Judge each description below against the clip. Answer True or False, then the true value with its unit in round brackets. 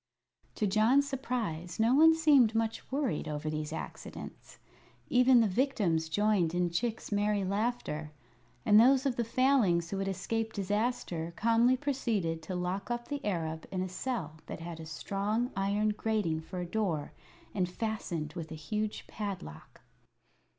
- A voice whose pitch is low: False (205 Hz)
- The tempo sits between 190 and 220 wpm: False (155 wpm)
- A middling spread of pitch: False (5.8 semitones)